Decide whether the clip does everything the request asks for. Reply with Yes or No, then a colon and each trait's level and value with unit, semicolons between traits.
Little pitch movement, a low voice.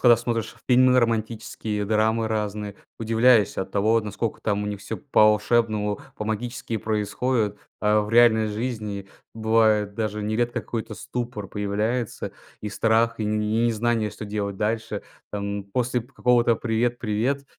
Yes: narrow, 1.9 semitones; low, 110 Hz